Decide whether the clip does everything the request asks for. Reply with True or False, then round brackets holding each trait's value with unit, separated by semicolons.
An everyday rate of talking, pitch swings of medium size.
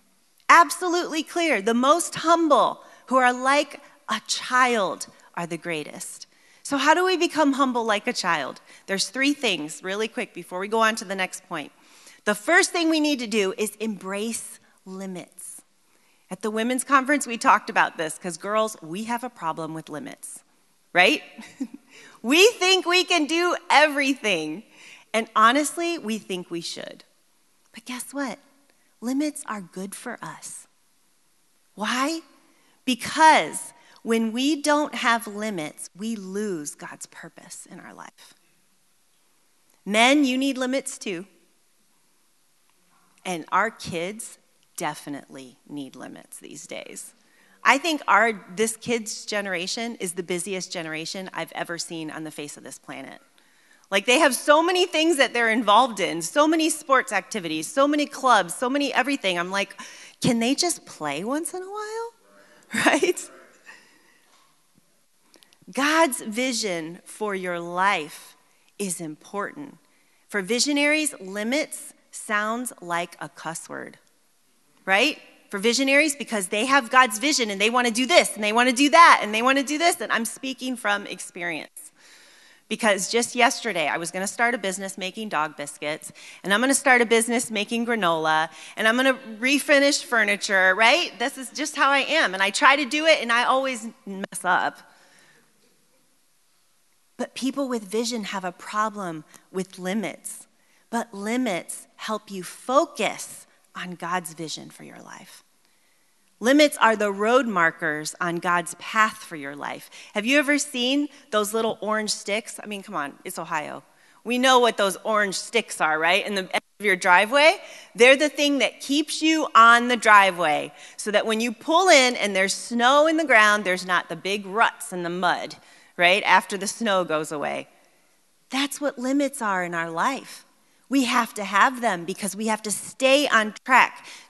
False (160 wpm; 6.5 semitones)